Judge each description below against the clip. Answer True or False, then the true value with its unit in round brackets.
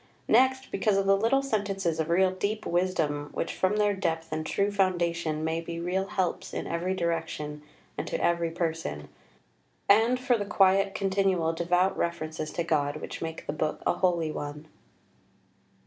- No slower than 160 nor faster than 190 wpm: True (165 wpm)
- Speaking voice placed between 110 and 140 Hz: False (175 Hz)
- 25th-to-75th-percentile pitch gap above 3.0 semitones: True (3.4 semitones)